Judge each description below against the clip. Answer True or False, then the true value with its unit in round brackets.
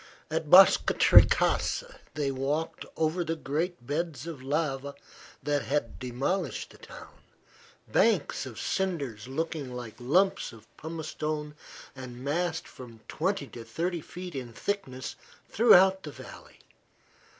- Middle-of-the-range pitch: True (150 Hz)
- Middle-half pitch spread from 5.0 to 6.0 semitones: False (4.5 semitones)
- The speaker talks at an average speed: False (125 wpm)